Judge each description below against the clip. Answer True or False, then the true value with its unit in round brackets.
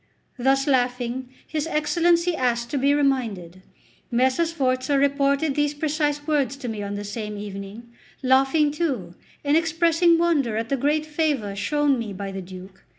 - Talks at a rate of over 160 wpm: False (155 wpm)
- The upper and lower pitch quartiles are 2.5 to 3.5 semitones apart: False (4.5 semitones)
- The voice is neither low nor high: False (270 Hz)